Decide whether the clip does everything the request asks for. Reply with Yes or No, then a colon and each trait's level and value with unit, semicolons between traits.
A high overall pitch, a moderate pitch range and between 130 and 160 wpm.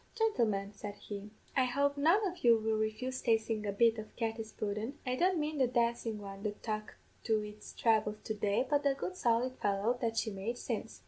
No: high, 225 Hz; average, 3.4 semitones; fast, 205 wpm